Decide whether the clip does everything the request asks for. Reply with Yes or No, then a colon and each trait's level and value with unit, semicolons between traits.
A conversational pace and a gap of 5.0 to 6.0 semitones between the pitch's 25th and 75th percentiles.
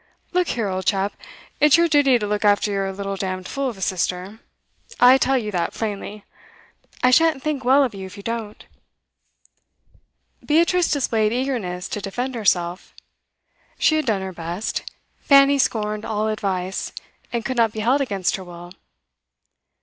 Yes: average, 165 wpm; wide, 5.4 semitones